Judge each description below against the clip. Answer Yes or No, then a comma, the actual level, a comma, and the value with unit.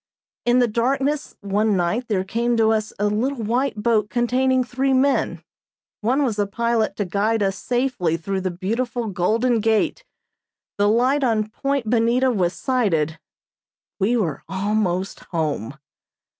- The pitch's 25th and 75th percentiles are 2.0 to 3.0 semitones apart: No, average, 3.9 semitones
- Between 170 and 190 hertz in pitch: No, high, 220 Hz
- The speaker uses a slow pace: No, average, 145 wpm